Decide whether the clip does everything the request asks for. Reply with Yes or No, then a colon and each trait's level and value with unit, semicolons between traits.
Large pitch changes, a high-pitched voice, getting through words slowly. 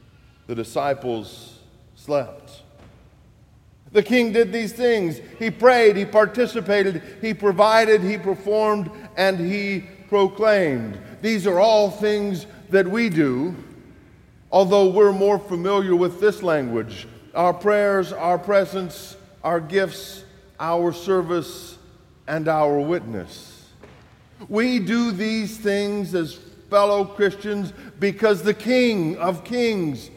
No: average, 4.1 semitones; high, 195 Hz; slow, 110 wpm